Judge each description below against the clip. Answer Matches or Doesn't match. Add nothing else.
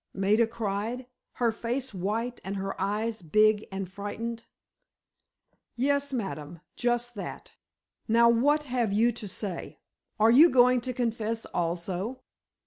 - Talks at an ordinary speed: Doesn't match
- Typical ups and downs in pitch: Matches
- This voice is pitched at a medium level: Doesn't match